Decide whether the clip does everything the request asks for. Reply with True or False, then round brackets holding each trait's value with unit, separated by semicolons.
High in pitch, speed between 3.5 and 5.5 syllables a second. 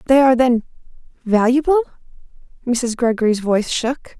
True (245 Hz; 5.3 syllables/s)